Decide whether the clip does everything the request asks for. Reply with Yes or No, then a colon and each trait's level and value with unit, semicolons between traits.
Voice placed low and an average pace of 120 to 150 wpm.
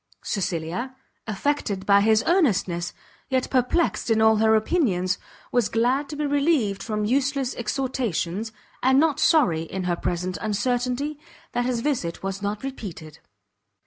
No: high, 225 Hz; average, 140 wpm